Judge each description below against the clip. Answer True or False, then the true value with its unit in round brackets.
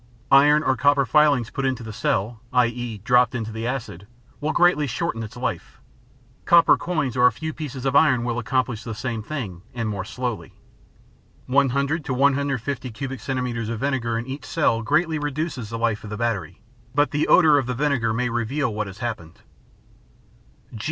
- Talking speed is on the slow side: False (180 wpm)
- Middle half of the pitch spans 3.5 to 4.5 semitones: True (3.8 semitones)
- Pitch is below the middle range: True (125 Hz)